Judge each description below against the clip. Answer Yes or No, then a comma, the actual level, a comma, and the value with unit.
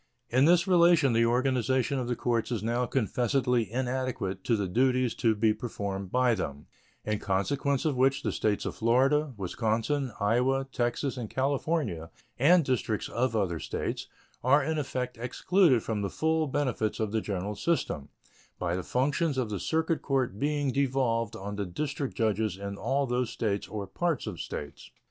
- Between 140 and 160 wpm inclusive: No, average, 170 wpm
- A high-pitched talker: No, low, 125 Hz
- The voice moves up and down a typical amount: Yes, average, 4.3 semitones